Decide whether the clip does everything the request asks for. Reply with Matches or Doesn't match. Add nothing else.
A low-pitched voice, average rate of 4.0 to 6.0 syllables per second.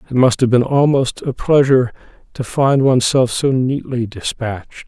Matches